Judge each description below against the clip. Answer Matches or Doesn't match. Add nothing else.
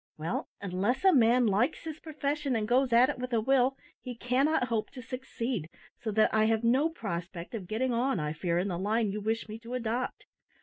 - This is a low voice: Doesn't match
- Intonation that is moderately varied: Matches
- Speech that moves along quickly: Matches